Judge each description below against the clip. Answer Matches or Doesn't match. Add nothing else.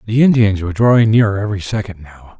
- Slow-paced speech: Doesn't match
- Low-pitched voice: Matches